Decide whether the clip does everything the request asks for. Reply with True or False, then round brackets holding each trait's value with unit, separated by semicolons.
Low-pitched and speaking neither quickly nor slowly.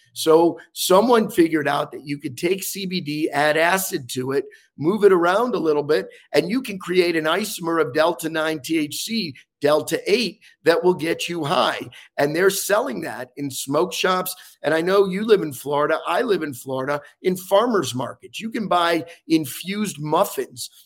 False (165 Hz; 180 wpm)